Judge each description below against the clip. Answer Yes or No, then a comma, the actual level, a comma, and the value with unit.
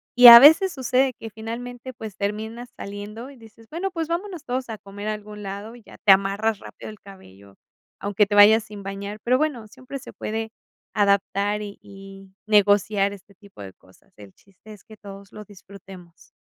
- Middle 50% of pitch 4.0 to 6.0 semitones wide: No, average, 3.0 semitones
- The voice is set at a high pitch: Yes, high, 210 Hz